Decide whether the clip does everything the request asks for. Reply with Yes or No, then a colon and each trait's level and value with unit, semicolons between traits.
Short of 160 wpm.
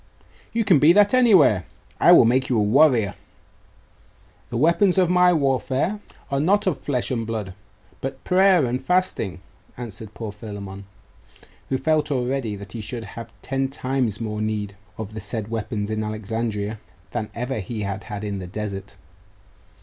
No: average, 165 wpm